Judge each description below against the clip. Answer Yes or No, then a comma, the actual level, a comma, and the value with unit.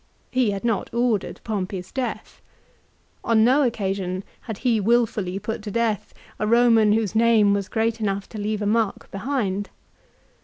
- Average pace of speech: Yes, average, 155 wpm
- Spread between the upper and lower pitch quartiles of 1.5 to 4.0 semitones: Yes, narrow, 2.5 semitones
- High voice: Yes, high, 215 Hz